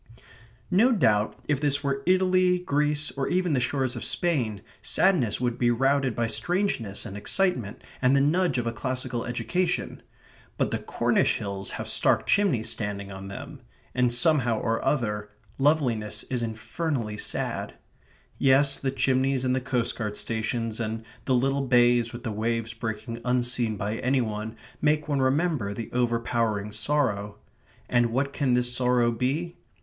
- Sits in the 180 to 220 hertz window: No, low, 125 Hz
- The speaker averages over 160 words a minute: No, average, 155 wpm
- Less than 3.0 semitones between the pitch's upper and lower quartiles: No, average, 4.0 semitones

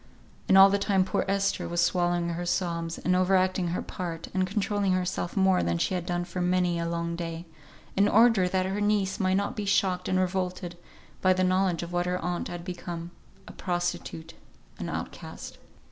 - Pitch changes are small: Yes, narrow, 1.6 semitones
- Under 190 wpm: No, average, 195 wpm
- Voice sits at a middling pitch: Yes, medium, 180 Hz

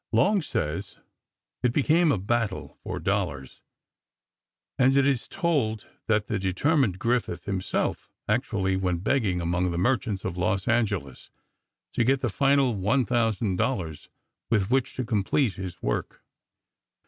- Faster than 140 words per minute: No, slow, 135 wpm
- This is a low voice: Yes, low, 110 Hz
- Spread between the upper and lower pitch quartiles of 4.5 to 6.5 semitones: Yes, wide, 5.5 semitones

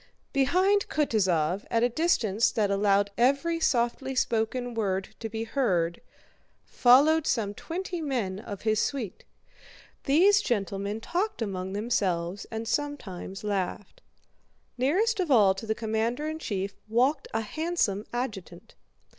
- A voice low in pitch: No, high, 225 Hz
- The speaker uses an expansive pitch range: Yes, wide, 5.9 semitones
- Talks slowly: Yes, slow, 130 wpm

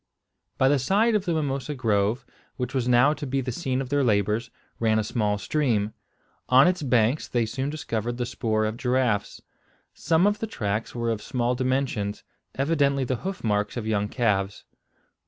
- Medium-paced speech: Yes, average, 180 wpm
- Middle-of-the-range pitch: No, low, 125 Hz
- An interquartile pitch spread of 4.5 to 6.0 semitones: No, average, 4.1 semitones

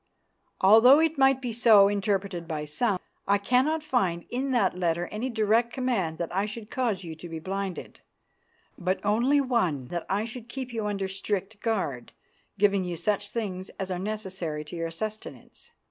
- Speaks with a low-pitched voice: No, high, 200 Hz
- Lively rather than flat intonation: No, average, 4.5 semitones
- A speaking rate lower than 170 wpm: No, average, 175 wpm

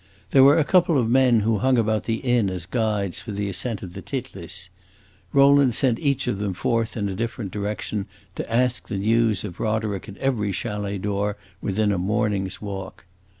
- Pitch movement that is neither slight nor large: Yes, average, 3.6 semitones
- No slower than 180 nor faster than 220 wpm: Yes, average, 195 wpm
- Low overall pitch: Yes, low, 105 Hz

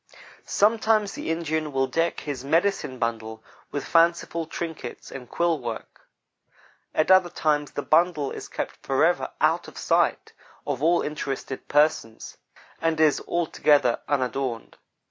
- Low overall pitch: No, medium, 155 Hz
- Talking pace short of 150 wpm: Yes, slow, 135 wpm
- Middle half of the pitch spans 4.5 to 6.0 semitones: No, average, 4.0 semitones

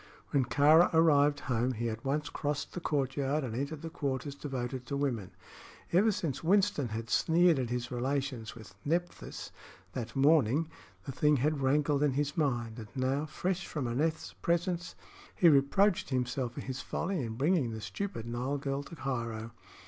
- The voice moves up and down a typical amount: Yes, average, 4.1 semitones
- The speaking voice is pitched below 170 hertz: Yes, medium, 140 Hz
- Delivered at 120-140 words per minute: No, average, 170 wpm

